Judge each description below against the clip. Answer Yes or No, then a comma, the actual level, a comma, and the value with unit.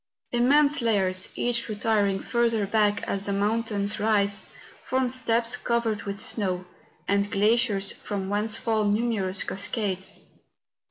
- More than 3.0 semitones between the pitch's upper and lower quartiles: No, average, 2.7 semitones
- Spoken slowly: Yes, slow, 125 wpm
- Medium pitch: No, high, 210 Hz